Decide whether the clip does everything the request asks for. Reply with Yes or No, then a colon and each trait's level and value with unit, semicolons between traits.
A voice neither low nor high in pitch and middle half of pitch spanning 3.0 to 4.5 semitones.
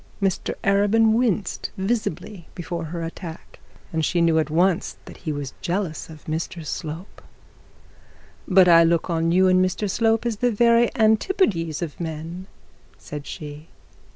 Yes: medium, 175 Hz; average, 4.1 semitones